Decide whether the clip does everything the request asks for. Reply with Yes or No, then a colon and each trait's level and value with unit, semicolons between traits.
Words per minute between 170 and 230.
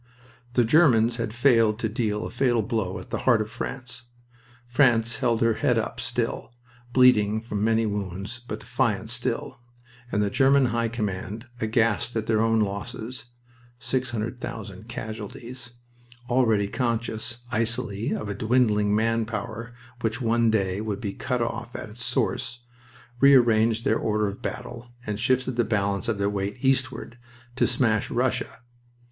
No: average, 155 wpm